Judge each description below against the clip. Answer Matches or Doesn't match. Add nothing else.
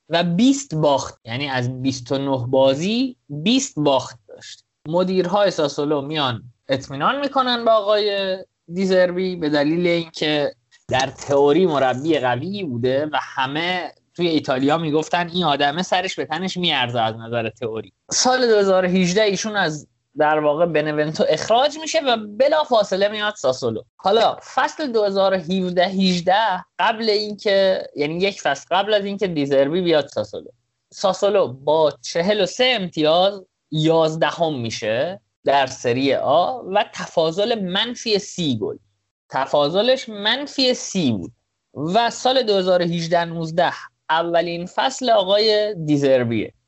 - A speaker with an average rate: Matches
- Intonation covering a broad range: Matches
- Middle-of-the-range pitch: Matches